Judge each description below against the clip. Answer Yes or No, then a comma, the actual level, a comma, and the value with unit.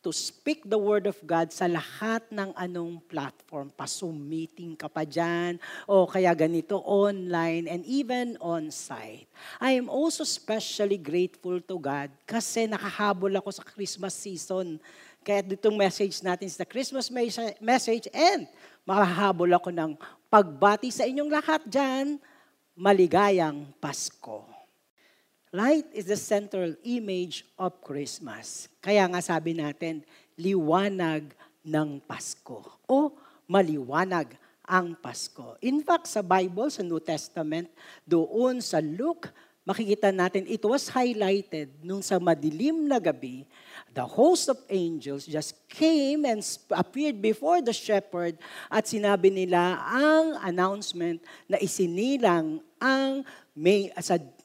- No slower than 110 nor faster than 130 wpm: Yes, average, 125 wpm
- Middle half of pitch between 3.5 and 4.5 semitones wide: No, wide, 5.4 semitones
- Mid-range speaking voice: No, high, 195 Hz